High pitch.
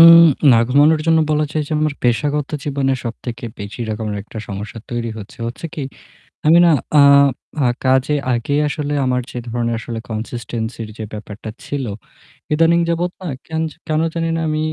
No: low, 135 Hz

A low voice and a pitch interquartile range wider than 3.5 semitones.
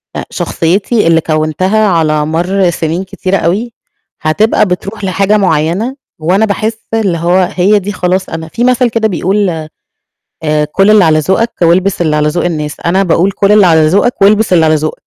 No: medium, 185 Hz; average, 4.1 semitones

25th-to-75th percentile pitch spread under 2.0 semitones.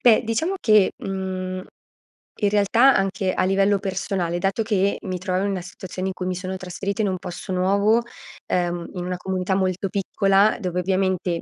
Yes: narrow, 1.5 semitones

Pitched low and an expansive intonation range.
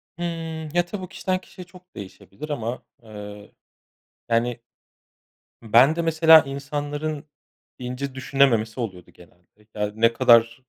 Yes: low, 130 Hz; wide, 6.1 semitones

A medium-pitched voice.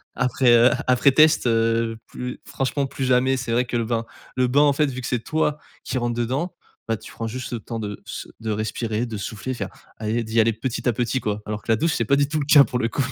No: low, 120 Hz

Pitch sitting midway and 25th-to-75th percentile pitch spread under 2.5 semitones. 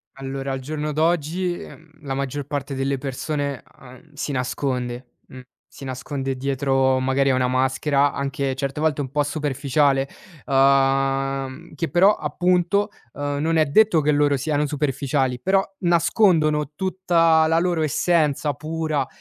No: medium, 145 Hz; average, 2.8 semitones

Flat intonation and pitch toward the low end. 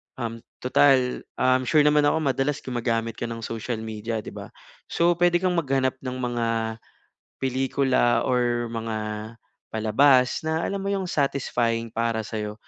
No: average, 3.4 semitones; low, 125 Hz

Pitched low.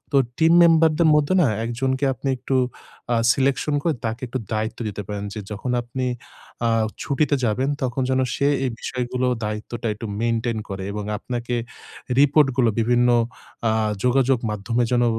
Yes: low, 125 Hz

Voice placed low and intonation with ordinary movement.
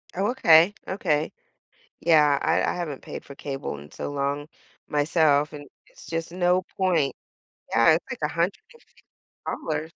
No: medium, 160 Hz; average, 3.6 semitones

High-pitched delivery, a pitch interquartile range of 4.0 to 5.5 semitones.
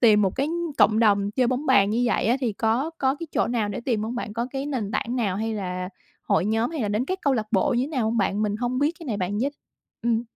No: high, 230 Hz; average, 3.6 semitones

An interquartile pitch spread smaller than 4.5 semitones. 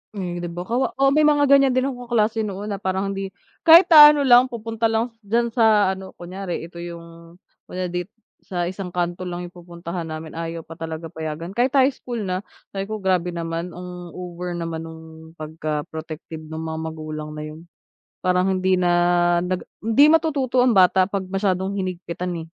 No: average, 4.8 semitones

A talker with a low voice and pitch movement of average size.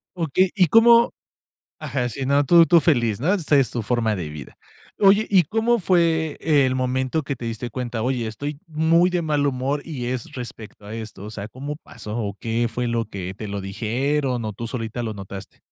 No: low, 130 Hz; wide, 6.0 semitones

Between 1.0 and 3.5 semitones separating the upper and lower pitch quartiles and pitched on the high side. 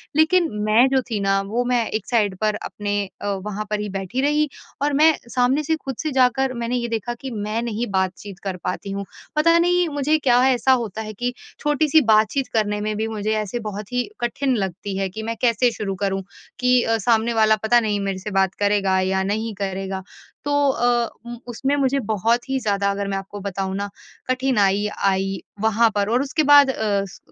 No: average, 4.3 semitones; high, 220 Hz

